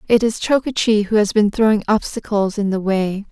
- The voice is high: Yes, high, 210 Hz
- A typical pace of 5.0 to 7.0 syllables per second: Yes, 5.2 syllables/s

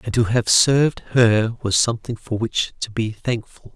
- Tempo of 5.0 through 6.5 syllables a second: No, 4.6 syllables/s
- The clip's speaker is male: Yes, male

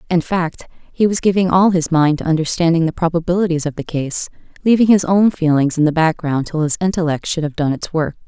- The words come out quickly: Yes, fast, 220 wpm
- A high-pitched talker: No, medium, 165 Hz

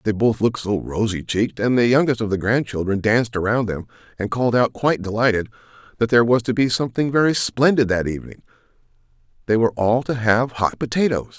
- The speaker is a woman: No, male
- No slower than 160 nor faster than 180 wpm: No, average, 190 wpm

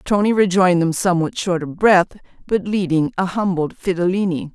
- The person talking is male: No, female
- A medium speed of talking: Yes, average, 160 wpm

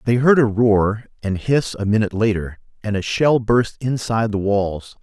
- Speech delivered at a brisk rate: No, average, 190 wpm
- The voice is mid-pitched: No, low, 110 Hz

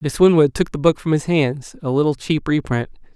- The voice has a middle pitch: Yes, medium, 150 Hz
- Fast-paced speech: Yes, fast, 210 wpm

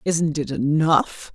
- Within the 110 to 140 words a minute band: Yes, slow, 135 wpm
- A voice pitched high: No, medium, 150 Hz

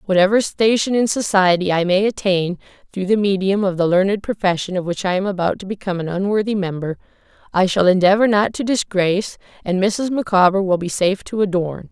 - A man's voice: No, female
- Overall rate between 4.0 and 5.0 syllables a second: No, 5.8 syllables/s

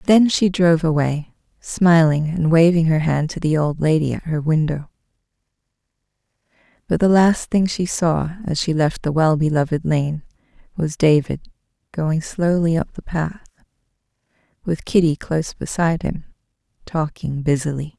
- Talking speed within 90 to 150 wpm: Yes, average, 145 wpm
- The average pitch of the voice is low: No, medium, 160 Hz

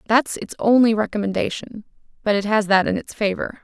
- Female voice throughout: Yes, female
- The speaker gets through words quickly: No, average, 180 wpm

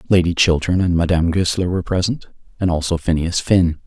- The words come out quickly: No, average, 170 wpm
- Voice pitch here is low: Yes, very low, 85 Hz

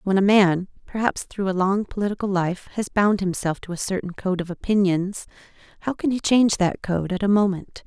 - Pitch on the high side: Yes, high, 195 Hz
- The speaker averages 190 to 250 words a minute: Yes, fast, 205 wpm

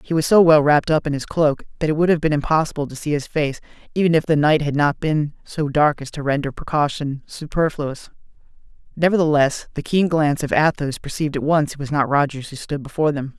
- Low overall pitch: No, medium, 150 Hz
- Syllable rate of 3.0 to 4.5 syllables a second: No, 6.0 syllables/s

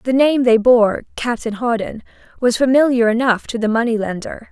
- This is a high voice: Yes, high, 235 Hz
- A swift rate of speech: No, average, 175 wpm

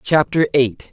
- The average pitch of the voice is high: No, medium, 140 Hz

